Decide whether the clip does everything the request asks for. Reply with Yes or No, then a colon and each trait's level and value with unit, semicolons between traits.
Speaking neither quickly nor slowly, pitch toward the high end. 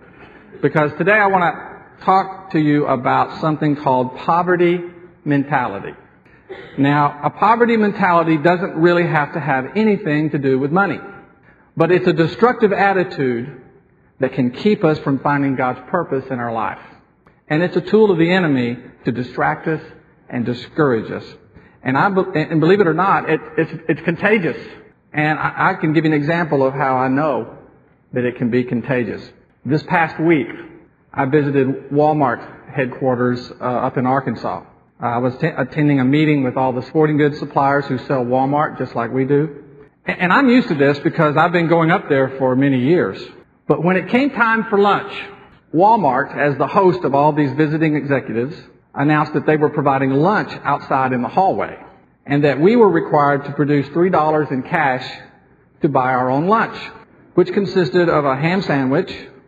No: average, 180 wpm; medium, 150 Hz